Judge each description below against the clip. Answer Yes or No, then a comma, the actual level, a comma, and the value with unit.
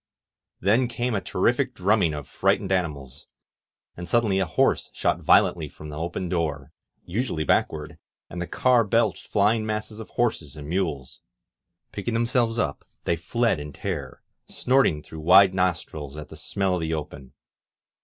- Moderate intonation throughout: No, wide, 6.5 semitones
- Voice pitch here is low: Yes, very low, 90 Hz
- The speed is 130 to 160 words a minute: Yes, average, 155 wpm